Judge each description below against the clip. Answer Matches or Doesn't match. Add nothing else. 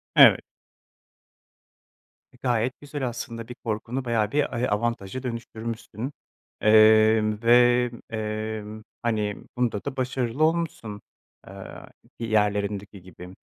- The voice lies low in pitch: Matches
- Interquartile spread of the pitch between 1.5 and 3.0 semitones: Matches